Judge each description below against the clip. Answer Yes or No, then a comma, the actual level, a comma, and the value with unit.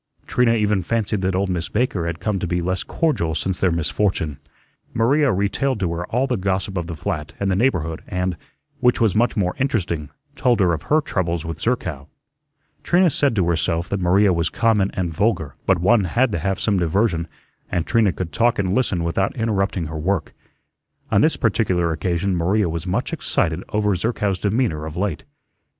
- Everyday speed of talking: Yes, average, 190 wpm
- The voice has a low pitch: Yes, very low, 95 Hz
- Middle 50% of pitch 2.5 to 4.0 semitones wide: No, average, 4.4 semitones